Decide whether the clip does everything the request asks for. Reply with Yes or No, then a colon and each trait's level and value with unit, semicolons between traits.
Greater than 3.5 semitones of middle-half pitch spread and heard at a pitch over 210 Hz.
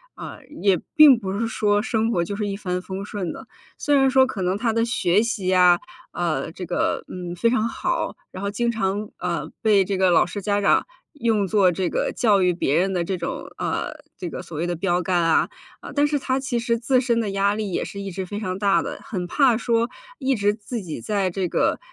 No: average, 4.0 semitones; high, 200 Hz